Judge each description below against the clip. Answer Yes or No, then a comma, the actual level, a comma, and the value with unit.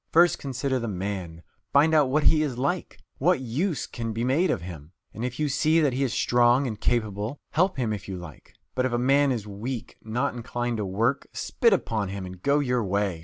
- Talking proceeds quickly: Yes, fast, 230 wpm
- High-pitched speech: No, low, 120 Hz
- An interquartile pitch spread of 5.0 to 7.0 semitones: Yes, average, 5.3 semitones